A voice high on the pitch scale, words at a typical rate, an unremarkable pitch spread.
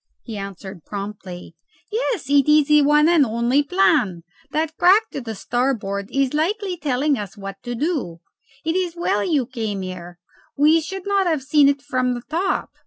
No: very high, 275 Hz; average, 175 wpm; wide, 7.2 semitones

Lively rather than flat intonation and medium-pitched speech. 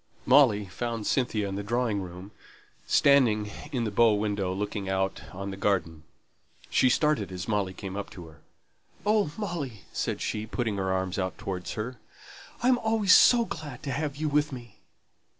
No: wide, 6.1 semitones; low, 105 Hz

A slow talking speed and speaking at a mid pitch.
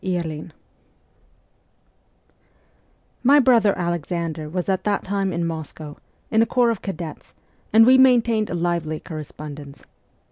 Yes: slow, 130 wpm; medium, 175 Hz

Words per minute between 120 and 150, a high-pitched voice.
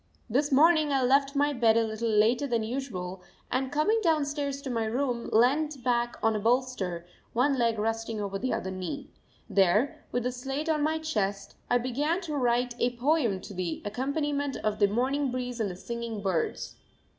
No: average, 185 wpm; high, 245 Hz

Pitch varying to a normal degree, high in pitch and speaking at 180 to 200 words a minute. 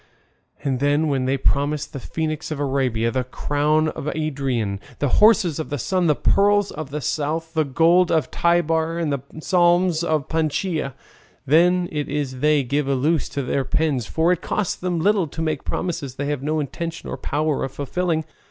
No: average, 3.0 semitones; medium, 155 Hz; average, 190 wpm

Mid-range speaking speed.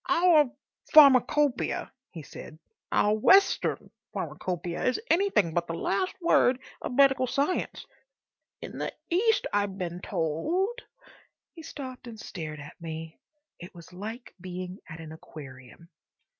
No: slow, 130 wpm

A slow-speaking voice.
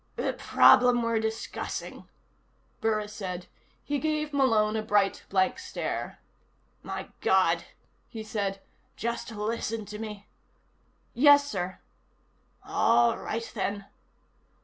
Yes: slow, 105 wpm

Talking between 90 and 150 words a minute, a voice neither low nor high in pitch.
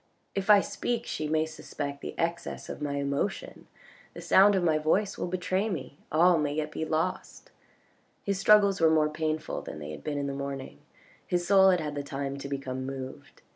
No: average, 200 wpm; medium, 155 Hz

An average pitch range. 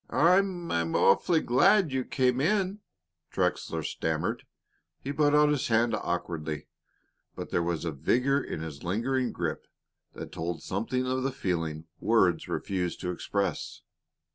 No: wide, 8.8 semitones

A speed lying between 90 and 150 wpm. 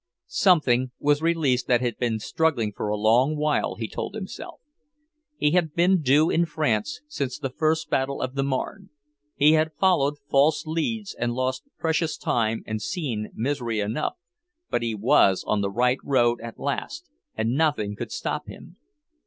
No: average, 170 wpm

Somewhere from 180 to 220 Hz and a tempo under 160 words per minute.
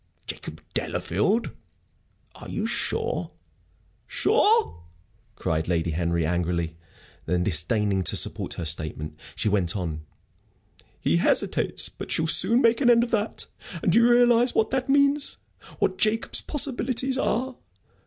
Yes: medium, 185 Hz; slow, 135 wpm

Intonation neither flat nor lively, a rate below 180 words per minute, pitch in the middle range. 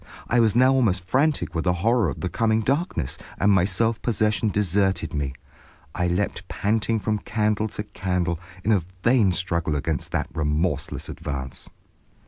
No: average, 4.3 semitones; average, 160 wpm; low, 100 Hz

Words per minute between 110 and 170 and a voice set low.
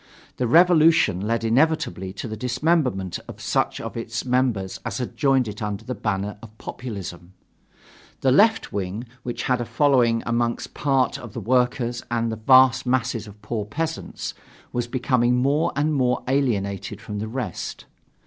Yes: average, 160 wpm; low, 120 Hz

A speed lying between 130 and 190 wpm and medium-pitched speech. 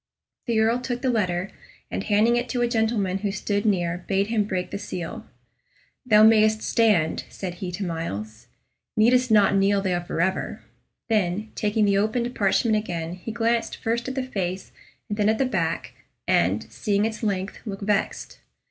No: average, 175 wpm; high, 210 Hz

